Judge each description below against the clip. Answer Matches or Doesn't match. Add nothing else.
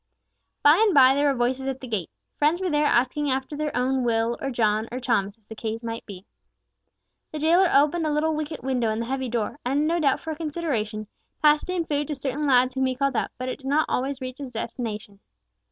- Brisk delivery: Matches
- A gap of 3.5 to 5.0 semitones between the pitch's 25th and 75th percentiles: Matches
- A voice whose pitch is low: Doesn't match